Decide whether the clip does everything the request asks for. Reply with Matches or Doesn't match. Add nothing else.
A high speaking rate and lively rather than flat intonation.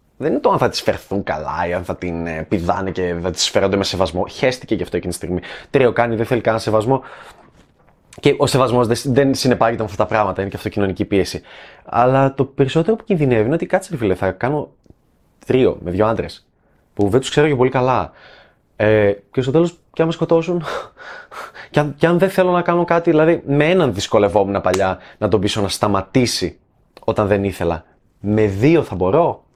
Matches